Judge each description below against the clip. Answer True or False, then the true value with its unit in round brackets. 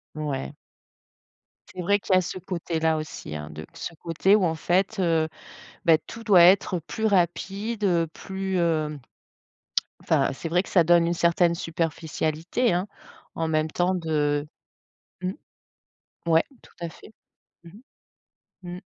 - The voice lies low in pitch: False (170 Hz)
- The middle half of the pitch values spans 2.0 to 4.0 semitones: True (2.7 semitones)